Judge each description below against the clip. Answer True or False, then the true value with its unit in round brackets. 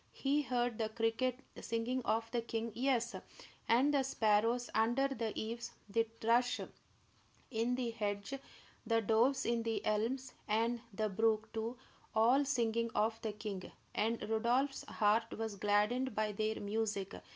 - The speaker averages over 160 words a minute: False (145 wpm)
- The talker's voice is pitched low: False (230 Hz)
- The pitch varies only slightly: True (2.0 semitones)